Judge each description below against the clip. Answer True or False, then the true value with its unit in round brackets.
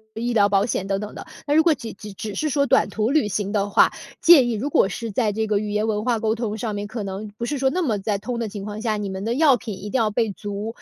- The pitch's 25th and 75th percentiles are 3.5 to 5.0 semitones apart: False (2.8 semitones)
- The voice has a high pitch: True (215 Hz)